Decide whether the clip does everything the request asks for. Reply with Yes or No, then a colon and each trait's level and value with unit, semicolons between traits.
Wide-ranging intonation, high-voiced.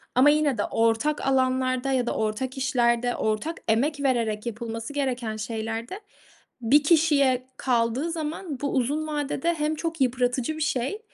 No: average, 4.1 semitones; very high, 260 Hz